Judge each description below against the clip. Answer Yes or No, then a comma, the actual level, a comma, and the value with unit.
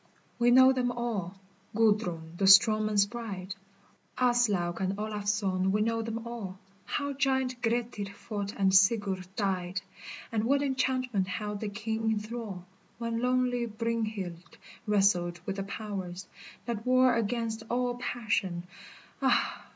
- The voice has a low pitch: No, high, 215 Hz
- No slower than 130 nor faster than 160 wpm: Yes, slow, 135 wpm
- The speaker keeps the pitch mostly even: No, average, 3.6 semitones